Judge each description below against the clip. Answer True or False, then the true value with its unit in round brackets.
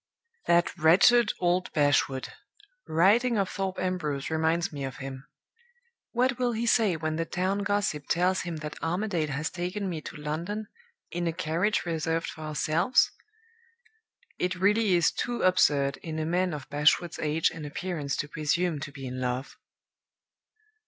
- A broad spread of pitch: False (3.7 semitones)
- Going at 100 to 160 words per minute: True (155 wpm)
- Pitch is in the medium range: True (170 Hz)